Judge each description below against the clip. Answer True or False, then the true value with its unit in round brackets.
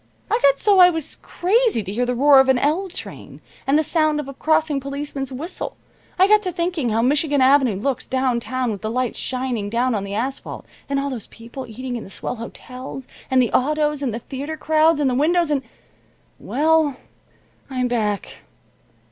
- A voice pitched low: False (270 Hz)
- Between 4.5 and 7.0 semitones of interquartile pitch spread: False (3.9 semitones)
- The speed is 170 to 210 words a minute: True (195 wpm)